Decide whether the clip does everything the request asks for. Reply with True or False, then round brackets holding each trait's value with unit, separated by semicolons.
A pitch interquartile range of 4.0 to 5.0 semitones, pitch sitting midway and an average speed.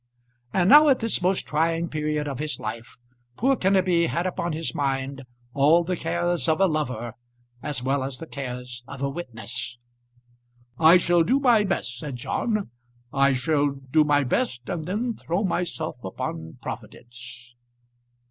False (5.4 semitones; 150 Hz; 155 wpm)